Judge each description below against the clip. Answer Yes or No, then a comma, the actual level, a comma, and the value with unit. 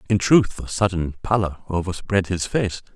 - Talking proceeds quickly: No, average, 160 wpm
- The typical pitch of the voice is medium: No, very low, 95 Hz